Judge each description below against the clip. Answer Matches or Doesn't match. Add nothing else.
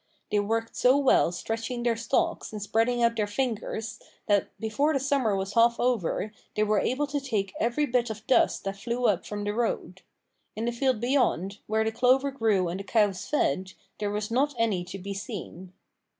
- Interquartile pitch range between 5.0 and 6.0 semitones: Doesn't match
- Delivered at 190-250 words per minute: Matches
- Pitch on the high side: Matches